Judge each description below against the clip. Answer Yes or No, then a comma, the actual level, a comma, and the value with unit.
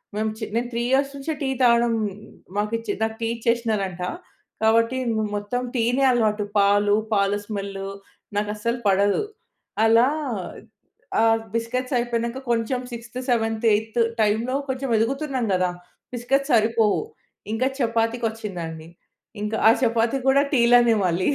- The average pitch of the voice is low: No, high, 230 Hz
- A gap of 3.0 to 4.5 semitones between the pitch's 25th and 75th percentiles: No, narrow, 2.4 semitones